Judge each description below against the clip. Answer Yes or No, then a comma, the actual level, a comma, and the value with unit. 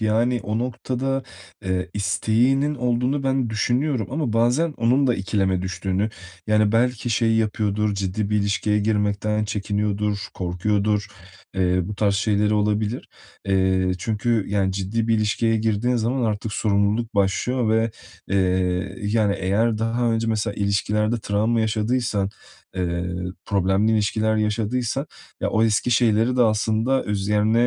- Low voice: Yes, low, 105 Hz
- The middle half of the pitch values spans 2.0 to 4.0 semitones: Yes, narrow, 2.4 semitones